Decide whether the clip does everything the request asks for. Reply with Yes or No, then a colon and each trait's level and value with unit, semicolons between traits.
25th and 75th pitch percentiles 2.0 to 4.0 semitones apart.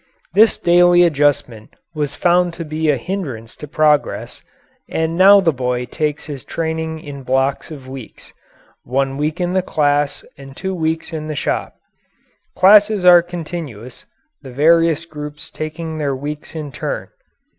Yes: average, 3.5 semitones